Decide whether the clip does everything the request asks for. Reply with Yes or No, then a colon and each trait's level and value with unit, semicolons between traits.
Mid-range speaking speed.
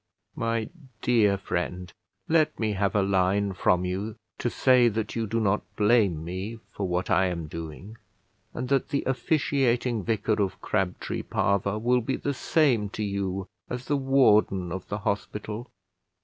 Yes: average, 160 wpm